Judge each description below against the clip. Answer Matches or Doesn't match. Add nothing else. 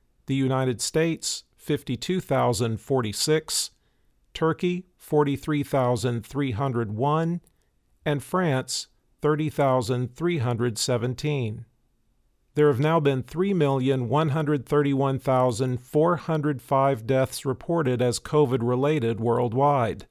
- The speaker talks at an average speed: Doesn't match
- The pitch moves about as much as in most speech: Matches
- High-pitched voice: Doesn't match